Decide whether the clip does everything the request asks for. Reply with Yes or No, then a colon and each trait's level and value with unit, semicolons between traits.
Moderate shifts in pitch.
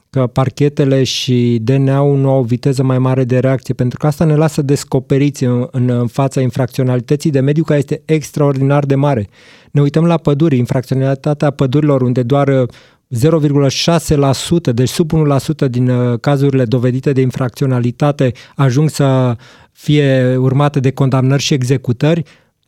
No: narrow, 2.3 semitones